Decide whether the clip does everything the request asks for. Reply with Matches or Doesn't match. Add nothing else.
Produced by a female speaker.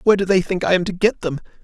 Doesn't match